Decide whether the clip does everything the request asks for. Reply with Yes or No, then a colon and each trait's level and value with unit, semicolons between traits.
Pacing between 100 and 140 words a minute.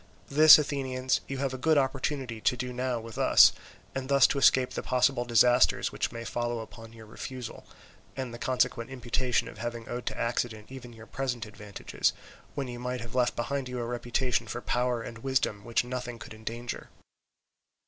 No: average, 185 wpm